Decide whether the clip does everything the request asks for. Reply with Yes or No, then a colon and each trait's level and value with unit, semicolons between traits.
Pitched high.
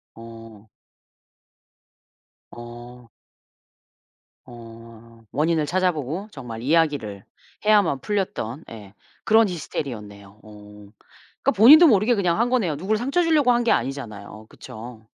No: low, 135 Hz